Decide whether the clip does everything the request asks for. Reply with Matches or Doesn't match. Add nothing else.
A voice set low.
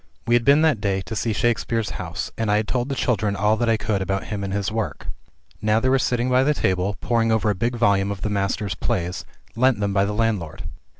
Matches